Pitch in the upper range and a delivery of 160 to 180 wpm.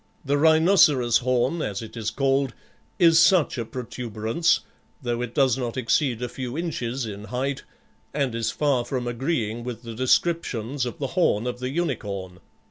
No: low, 125 Hz; average, 165 wpm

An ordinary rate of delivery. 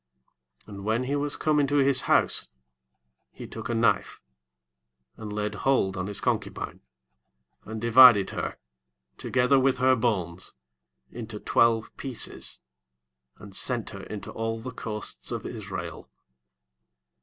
No: slow, 130 wpm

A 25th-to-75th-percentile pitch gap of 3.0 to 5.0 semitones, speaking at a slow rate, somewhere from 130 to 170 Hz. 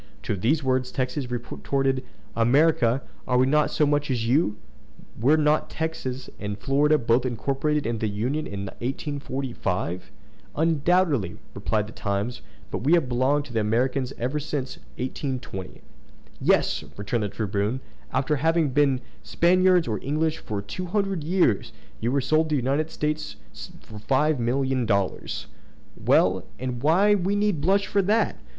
No: average, 4.6 semitones; average, 155 wpm; low, 135 Hz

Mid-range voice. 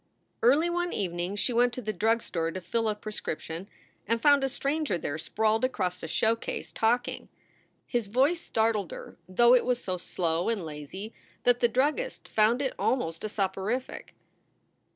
No: high, 225 Hz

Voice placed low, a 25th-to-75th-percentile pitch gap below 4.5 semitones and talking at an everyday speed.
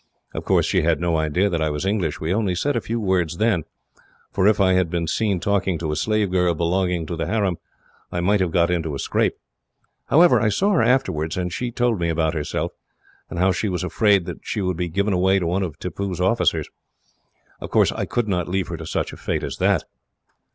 No: very low, 90 Hz; average, 3.3 semitones; fast, 230 wpm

